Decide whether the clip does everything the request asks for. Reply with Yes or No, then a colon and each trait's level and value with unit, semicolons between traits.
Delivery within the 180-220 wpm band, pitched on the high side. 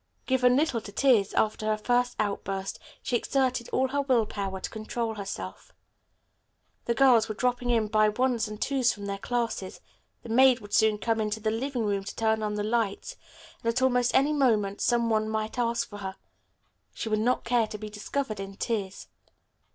Yes: average, 190 wpm; high, 225 Hz